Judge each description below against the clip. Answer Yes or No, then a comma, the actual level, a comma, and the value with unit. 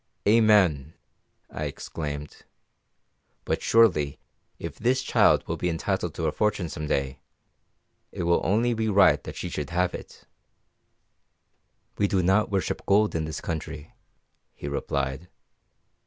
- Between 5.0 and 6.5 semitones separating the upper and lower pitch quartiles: Yes, wide, 5.4 semitones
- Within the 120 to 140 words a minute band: Yes, slow, 135 wpm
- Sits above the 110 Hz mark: No, very low, 85 Hz